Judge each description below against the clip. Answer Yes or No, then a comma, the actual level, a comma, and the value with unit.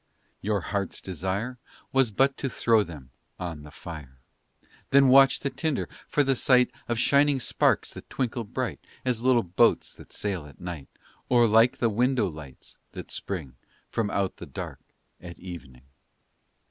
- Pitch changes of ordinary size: No, wide, 6.8 semitones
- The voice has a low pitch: Yes, low, 105 Hz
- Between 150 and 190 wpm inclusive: Yes, average, 160 wpm